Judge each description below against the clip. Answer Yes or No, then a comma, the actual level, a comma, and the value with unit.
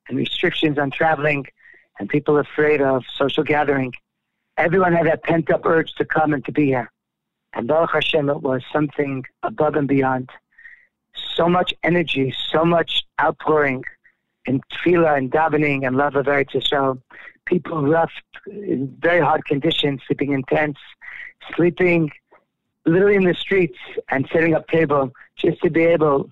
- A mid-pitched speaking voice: Yes, medium, 150 Hz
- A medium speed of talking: Yes, average, 155 wpm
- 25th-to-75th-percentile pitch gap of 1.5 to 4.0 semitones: Yes, average, 3.2 semitones